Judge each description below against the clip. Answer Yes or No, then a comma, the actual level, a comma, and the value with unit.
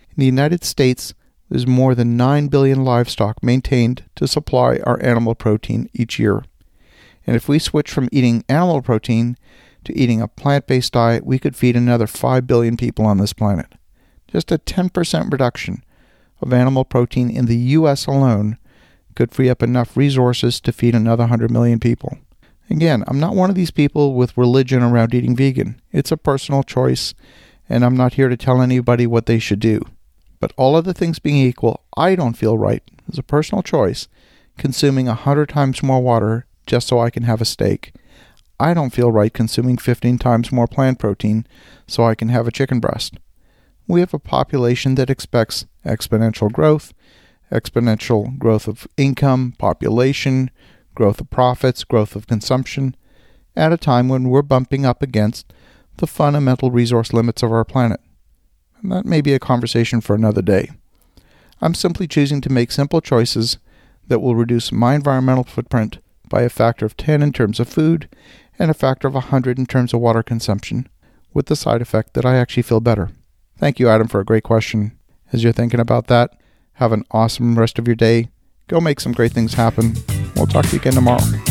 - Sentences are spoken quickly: No, average, 185 wpm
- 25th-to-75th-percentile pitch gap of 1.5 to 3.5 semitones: Yes, average, 2.9 semitones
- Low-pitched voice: Yes, low, 120 Hz